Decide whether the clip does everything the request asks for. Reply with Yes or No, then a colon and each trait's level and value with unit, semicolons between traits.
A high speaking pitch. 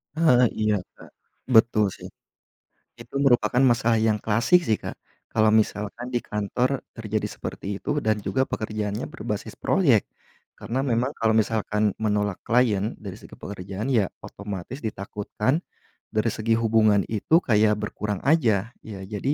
No: low, 110 Hz